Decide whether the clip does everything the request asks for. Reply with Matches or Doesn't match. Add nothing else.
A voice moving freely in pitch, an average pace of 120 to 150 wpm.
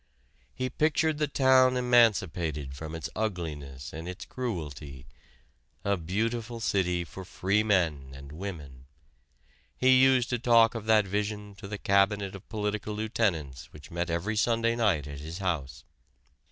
Matches